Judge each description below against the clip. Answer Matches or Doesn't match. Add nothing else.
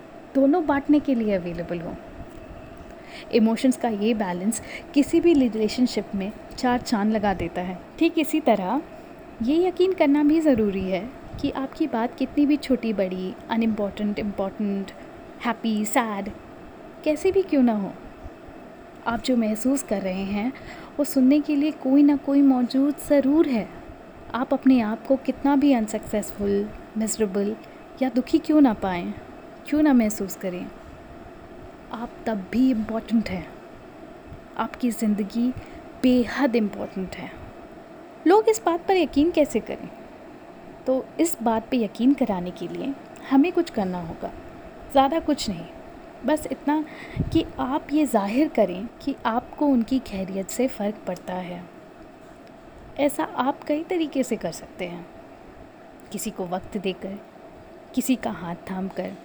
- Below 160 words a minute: Matches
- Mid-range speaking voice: Doesn't match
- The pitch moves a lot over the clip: Matches